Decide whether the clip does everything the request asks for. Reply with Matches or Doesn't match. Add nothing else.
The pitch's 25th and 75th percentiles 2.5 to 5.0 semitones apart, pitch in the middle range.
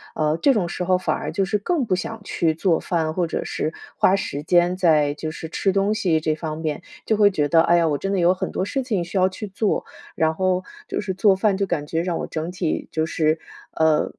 Matches